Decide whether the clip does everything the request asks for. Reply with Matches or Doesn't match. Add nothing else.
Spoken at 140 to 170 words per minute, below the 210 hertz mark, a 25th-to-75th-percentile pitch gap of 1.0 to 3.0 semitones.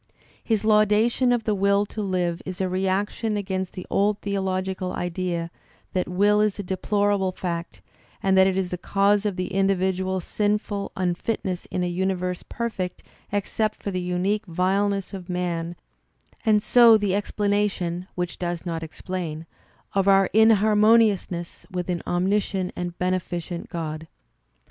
Matches